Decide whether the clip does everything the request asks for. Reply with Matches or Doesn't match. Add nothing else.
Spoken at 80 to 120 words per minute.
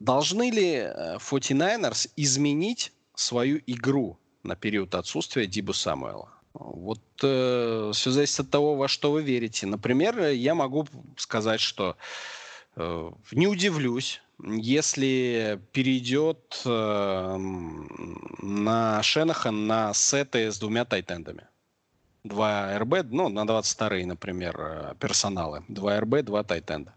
Matches